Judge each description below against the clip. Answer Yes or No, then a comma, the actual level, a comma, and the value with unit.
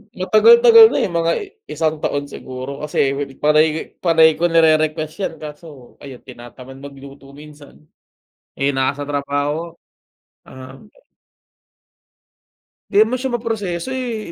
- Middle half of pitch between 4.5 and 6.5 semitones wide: No, average, 3.6 semitones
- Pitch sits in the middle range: Yes, medium, 155 Hz